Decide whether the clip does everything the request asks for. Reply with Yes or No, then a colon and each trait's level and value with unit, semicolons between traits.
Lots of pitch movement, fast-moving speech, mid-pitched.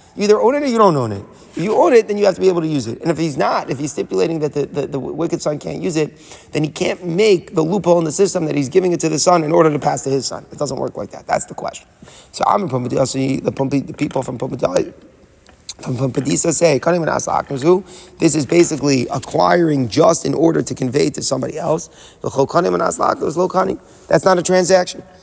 No: average, 4.3 semitones; fast, 235 wpm; medium, 165 Hz